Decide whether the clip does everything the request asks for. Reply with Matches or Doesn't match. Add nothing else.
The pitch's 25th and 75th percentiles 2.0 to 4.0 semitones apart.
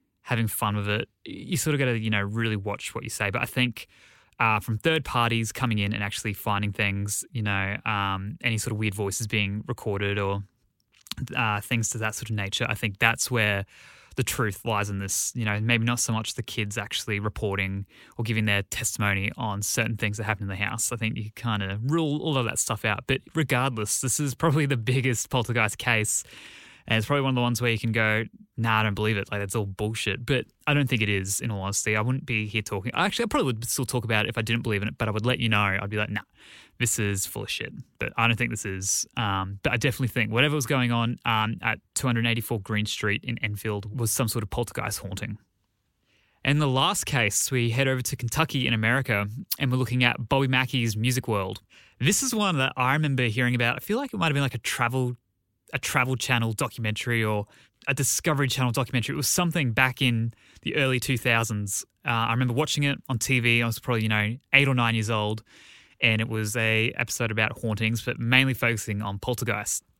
Matches